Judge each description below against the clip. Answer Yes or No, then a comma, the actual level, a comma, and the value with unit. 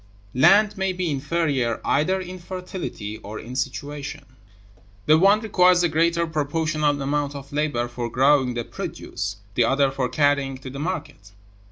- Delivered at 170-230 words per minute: No, average, 155 wpm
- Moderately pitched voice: Yes, medium, 145 Hz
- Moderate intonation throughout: Yes, average, 4.5 semitones